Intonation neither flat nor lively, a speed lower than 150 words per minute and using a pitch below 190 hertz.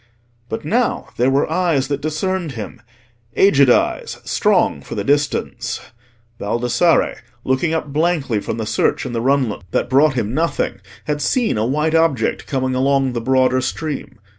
No: average, 4.2 semitones; average, 155 wpm; low, 135 Hz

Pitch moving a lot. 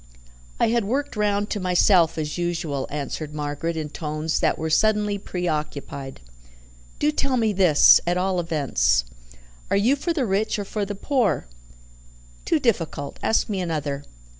Yes: wide, 5.7 semitones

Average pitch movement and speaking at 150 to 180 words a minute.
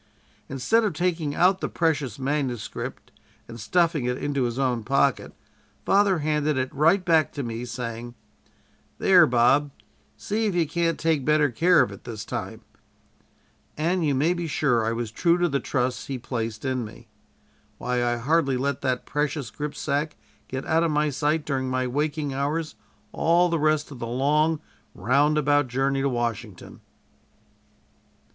Yes: average, 4.1 semitones; average, 160 wpm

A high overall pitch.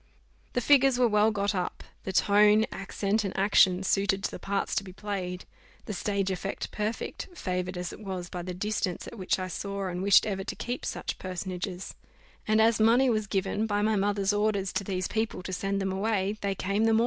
Yes: high, 200 Hz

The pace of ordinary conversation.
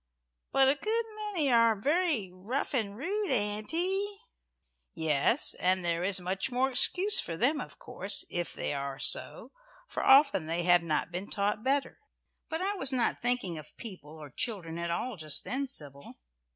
Yes: average, 170 wpm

